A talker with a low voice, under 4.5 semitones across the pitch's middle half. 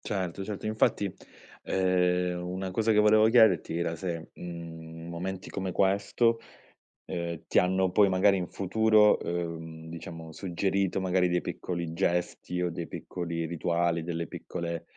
Yes: very low, 90 Hz; narrow, 2.4 semitones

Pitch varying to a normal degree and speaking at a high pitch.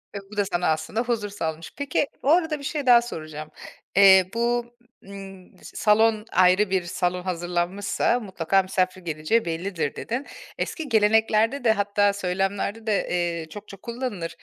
Yes: average, 4.0 semitones; high, 200 Hz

